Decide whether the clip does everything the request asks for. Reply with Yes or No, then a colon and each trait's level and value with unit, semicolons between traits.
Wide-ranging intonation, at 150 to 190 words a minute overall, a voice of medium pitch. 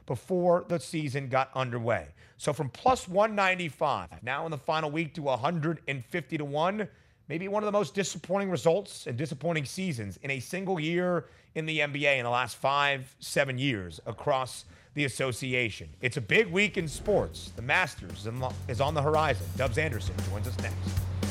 Yes: wide, 6.3 semitones; average, 170 wpm; medium, 145 Hz